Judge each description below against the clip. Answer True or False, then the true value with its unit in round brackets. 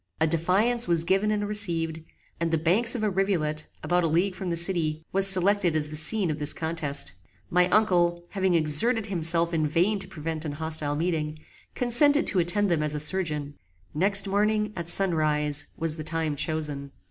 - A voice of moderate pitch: True (170 Hz)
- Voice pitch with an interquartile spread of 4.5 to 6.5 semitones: False (3.9 semitones)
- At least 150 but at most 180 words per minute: False (190 wpm)